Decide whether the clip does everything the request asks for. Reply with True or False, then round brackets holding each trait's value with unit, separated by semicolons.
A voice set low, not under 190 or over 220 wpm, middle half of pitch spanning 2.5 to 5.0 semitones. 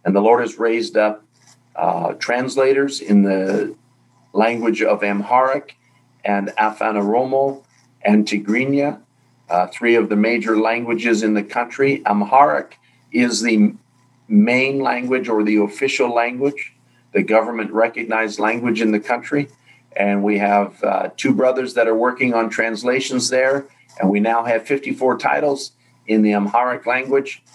False (120 Hz; 140 wpm; 3.1 semitones)